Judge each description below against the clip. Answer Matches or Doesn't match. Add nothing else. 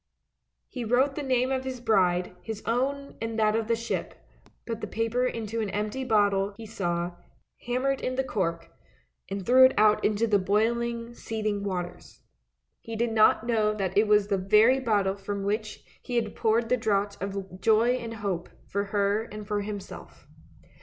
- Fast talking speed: Doesn't match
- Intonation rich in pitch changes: Doesn't match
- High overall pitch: Matches